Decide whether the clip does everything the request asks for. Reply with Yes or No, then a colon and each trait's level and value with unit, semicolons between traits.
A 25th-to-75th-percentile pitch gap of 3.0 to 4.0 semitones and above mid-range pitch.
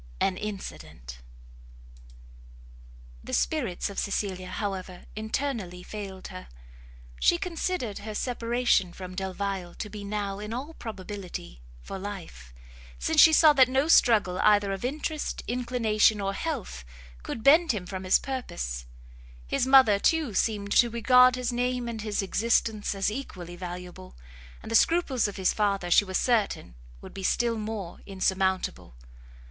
No: average, 4.6 semitones; high, 210 Hz